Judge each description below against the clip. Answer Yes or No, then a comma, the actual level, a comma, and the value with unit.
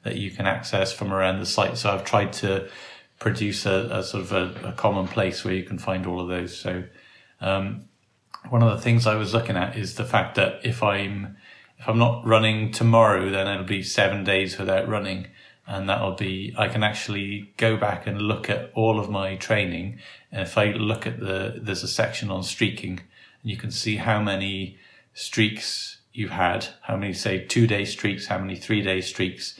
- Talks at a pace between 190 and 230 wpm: Yes, fast, 205 wpm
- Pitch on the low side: Yes, low, 100 Hz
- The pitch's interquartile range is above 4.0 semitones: No, narrow, 2.4 semitones